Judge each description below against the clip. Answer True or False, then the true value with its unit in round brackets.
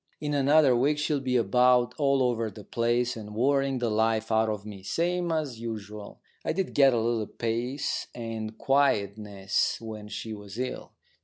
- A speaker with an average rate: True (170 wpm)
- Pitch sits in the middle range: False (120 Hz)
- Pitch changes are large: False (3.9 semitones)